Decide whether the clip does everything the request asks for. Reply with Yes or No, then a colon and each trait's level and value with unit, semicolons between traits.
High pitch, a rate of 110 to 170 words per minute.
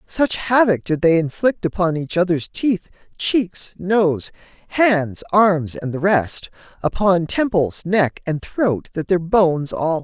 No: medium, 180 Hz; average, 155 wpm